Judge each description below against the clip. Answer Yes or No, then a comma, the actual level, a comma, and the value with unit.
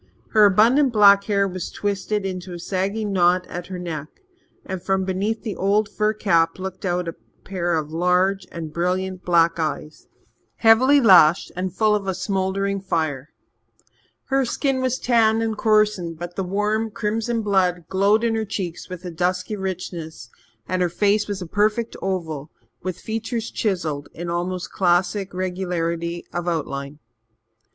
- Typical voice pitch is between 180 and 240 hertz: Yes, high, 190 Hz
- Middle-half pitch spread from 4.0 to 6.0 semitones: No, average, 3.3 semitones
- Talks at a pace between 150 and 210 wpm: Yes, average, 160 wpm